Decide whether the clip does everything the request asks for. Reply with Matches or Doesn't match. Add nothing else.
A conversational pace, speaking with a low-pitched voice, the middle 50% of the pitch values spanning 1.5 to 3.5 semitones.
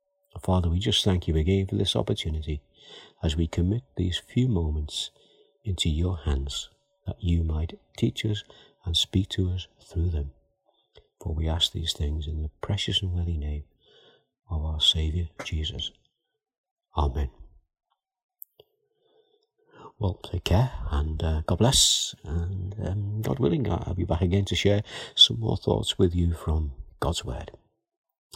Doesn't match